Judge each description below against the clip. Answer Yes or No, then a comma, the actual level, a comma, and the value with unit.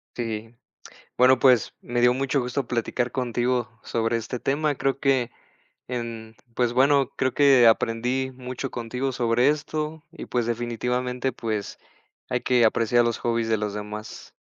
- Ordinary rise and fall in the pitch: No, narrow, 2.3 semitones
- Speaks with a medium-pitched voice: No, low, 125 Hz